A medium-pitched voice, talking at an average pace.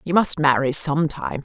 Yes: medium, 145 Hz; average, 165 wpm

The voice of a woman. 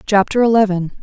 Yes: female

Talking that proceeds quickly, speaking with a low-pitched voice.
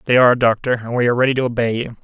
Yes: fast, 295 wpm; low, 120 Hz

